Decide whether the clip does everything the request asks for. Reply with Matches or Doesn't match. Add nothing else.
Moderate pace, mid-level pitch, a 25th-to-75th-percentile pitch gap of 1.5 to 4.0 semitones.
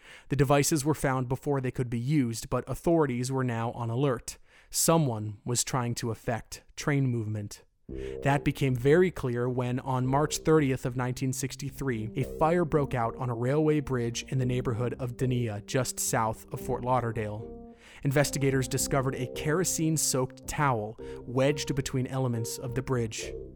Doesn't match